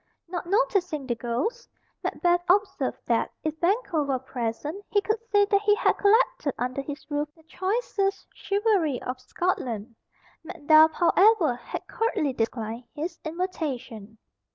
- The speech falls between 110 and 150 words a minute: Yes, slow, 135 wpm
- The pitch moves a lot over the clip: Yes, wide, 7.5 semitones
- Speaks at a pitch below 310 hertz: No, very high, 320 Hz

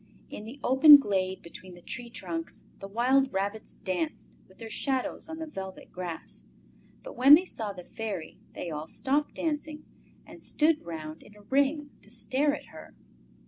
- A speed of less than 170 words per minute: No, average, 175 wpm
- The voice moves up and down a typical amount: No, wide, 7.3 semitones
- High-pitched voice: Yes, high, 230 Hz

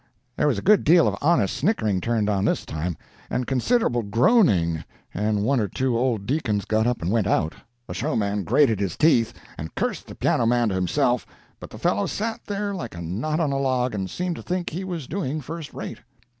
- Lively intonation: Yes, wide, 7.4 semitones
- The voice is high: No, low, 120 Hz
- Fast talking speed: Yes, fast, 210 wpm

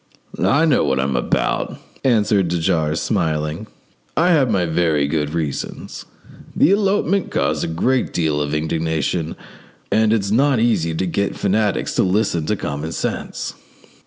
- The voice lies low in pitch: Yes, very low, 85 Hz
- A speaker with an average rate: Yes, average, 150 wpm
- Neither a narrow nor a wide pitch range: No, wide, 6.1 semitones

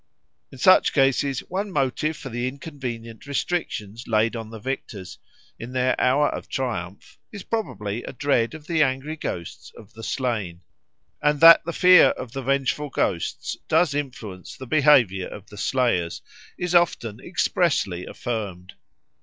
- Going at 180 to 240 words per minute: No, average, 150 wpm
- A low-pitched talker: Yes, low, 130 Hz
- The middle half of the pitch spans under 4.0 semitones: No, average, 5.1 semitones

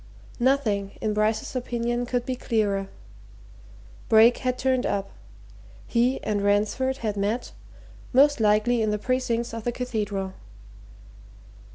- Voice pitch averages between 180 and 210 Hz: No, high, 230 Hz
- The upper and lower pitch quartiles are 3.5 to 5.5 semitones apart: No, average, 3.0 semitones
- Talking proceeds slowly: Yes, slow, 125 wpm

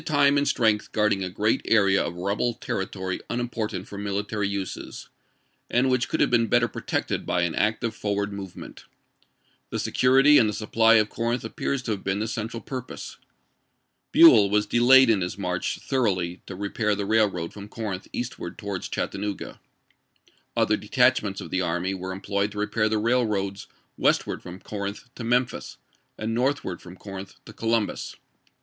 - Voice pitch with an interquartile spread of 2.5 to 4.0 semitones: Yes, average, 3.0 semitones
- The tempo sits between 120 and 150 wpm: No, average, 170 wpm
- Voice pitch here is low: Yes, low, 105 Hz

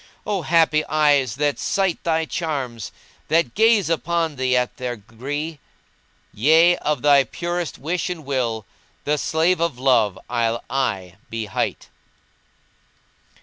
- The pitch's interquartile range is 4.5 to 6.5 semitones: Yes, average, 5.0 semitones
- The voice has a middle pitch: Yes, medium, 145 Hz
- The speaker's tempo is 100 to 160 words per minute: Yes, average, 140 wpm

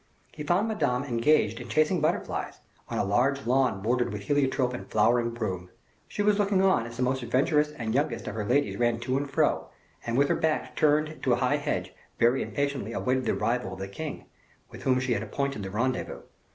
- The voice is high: No, low, 130 Hz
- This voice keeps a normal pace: No, fast, 210 wpm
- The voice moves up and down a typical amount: Yes, average, 3.9 semitones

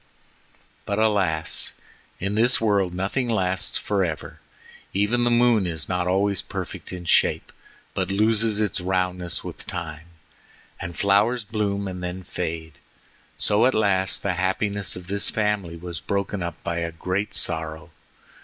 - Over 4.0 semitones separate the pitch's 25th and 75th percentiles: No, average, 3.0 semitones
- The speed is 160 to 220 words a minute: No, average, 145 wpm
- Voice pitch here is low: Yes, very low, 95 Hz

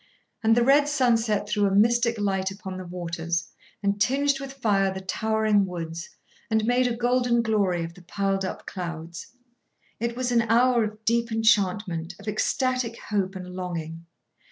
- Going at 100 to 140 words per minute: No, average, 165 wpm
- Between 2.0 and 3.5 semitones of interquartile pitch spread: No, average, 4.1 semitones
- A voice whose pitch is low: No, high, 210 Hz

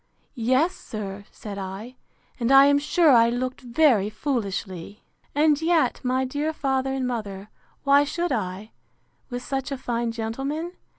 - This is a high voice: Yes, very high, 255 Hz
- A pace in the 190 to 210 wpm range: No, average, 145 wpm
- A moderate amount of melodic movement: Yes, average, 4.5 semitones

